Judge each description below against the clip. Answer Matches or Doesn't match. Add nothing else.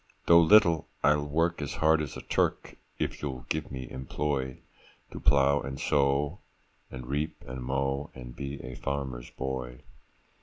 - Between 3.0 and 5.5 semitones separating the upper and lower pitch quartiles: Doesn't match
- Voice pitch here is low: Matches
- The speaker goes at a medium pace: Matches